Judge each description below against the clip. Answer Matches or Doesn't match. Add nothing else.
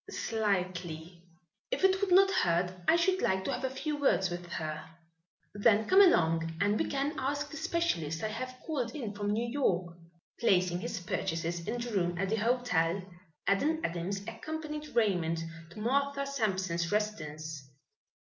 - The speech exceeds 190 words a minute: Doesn't match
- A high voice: Matches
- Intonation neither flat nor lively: Doesn't match